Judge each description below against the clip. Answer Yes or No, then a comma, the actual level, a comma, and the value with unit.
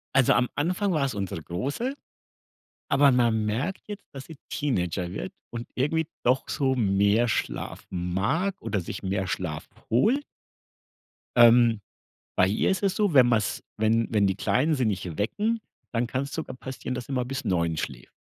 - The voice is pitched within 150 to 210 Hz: No, low, 120 Hz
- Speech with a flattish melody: No, wide, 6.1 semitones